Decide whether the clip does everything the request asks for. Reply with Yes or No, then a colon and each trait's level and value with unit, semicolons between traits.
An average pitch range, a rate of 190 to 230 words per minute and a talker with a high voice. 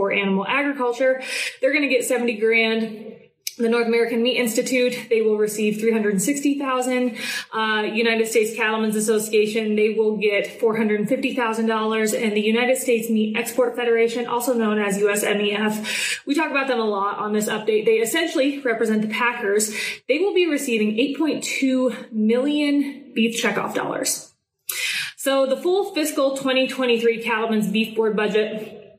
No: average, 3.1 semitones; average, 170 wpm; high, 230 Hz